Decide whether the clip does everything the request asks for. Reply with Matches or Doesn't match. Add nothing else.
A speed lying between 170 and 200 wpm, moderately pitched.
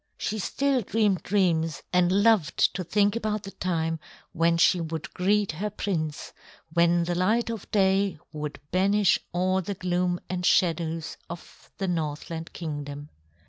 Doesn't match